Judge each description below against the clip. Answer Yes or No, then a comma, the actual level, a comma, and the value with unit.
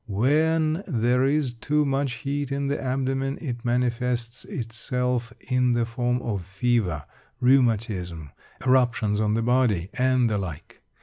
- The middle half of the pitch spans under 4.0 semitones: Yes, average, 2.7 semitones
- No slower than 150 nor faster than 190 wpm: No, slow, 135 wpm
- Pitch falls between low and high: No, low, 125 Hz